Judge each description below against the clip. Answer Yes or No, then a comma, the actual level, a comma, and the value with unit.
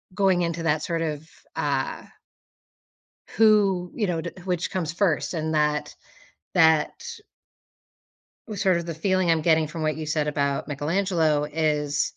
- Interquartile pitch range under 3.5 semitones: Yes, average, 2.8 semitones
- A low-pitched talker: No, medium, 165 Hz